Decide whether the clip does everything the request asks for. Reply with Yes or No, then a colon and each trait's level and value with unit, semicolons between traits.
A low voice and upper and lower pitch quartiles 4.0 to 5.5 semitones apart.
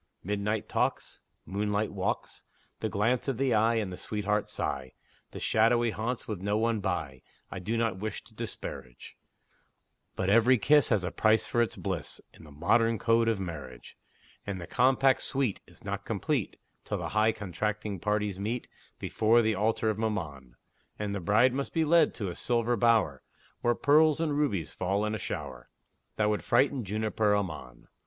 No: low, 105 Hz; average, 3.1 semitones